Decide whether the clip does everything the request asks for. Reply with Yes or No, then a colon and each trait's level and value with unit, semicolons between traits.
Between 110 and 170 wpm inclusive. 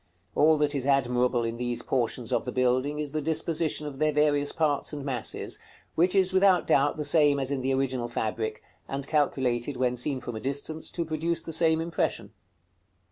No: average, 190 wpm